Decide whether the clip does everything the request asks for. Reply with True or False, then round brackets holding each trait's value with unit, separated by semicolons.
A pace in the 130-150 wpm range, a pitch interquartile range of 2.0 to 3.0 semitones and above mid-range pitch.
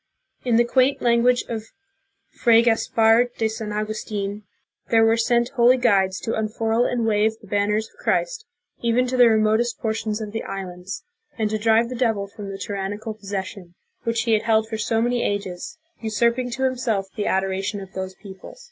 False (185 wpm; 2.5 semitones; 220 Hz)